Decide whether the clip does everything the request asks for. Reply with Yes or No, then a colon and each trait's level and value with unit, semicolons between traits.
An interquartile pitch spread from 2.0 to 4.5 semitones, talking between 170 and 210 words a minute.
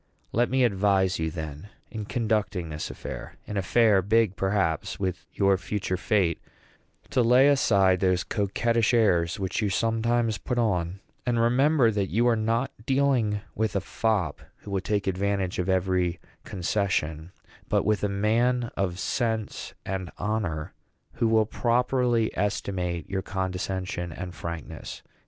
No: average, 3.8 semitones; average, 145 wpm